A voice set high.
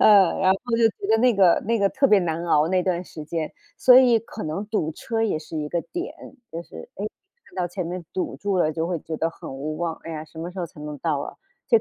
No: medium, 175 Hz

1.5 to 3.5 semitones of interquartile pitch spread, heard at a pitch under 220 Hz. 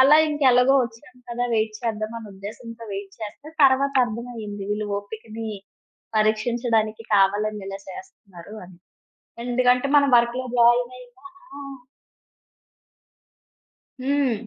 No: average, 2.7 semitones; high, 230 Hz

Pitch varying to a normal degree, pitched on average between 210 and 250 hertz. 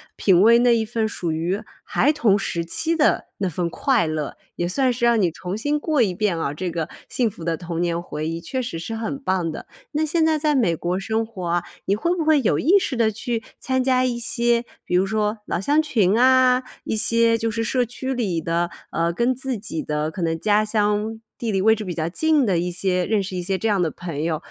No: wide, 5.9 semitones; high, 215 Hz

